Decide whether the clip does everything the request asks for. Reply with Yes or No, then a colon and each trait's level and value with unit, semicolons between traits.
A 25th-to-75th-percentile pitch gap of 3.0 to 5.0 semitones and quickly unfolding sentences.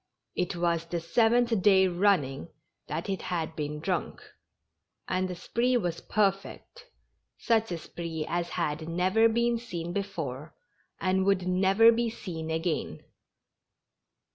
No: average, 4.0 semitones; slow, 135 wpm